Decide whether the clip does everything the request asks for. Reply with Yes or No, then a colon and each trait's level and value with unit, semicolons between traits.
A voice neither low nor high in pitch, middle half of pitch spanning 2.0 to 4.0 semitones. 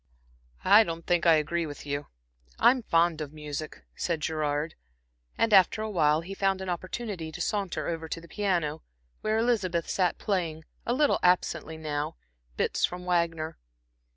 Yes: medium, 170 Hz; average, 3.6 semitones